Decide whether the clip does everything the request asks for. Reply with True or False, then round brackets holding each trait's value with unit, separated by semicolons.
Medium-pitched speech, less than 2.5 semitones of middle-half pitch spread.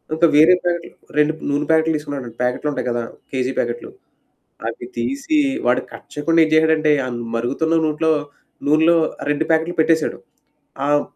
True (155 Hz; 2.1 semitones)